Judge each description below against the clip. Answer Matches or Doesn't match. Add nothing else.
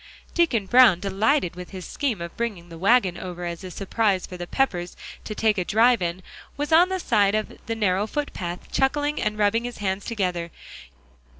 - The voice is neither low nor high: Doesn't match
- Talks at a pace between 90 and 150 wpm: Doesn't match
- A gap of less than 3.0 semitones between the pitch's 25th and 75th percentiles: Doesn't match